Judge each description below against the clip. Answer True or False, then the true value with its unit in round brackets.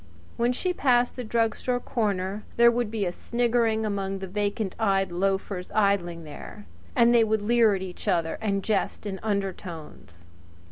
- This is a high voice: True (205 Hz)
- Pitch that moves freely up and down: False (3.4 semitones)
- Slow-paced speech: False (170 wpm)